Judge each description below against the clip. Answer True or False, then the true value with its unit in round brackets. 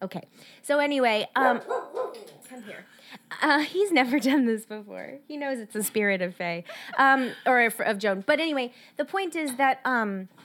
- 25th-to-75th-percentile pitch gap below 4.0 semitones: False (5.4 semitones)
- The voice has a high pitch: True (255 Hz)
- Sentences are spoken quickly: False (170 wpm)